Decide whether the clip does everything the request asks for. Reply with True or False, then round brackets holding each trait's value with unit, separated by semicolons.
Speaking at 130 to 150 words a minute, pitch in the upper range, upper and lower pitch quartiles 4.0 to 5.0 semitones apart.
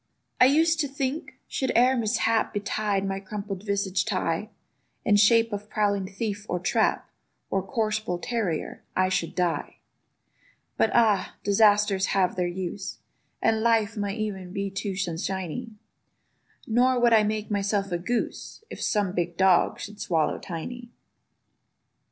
False (140 wpm; 205 Hz; 2.9 semitones)